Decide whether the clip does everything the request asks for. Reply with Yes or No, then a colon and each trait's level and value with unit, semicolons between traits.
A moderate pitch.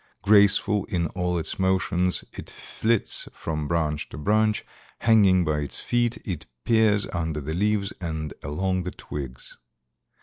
No: very low, 90 Hz